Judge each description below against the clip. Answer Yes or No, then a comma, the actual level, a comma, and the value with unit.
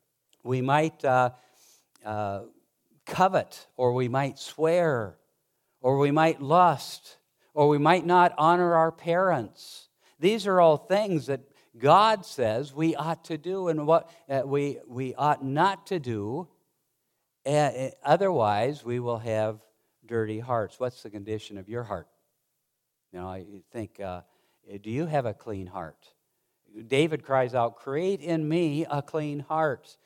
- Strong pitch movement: Yes, wide, 5.8 semitones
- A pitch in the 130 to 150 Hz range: Yes, medium, 140 Hz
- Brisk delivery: No, average, 145 wpm